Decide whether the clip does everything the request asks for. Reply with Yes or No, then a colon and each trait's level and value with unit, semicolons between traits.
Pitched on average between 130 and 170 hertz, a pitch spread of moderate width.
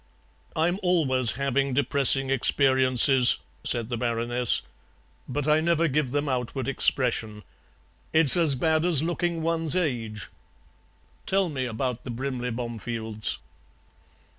Yes: low, 135 Hz; average, 4.5 semitones